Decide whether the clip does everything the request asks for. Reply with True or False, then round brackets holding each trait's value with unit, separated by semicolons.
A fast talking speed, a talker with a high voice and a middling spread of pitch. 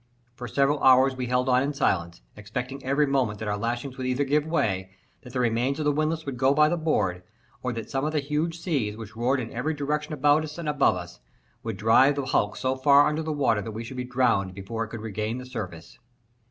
False (240 wpm; 130 Hz; 4.5 semitones)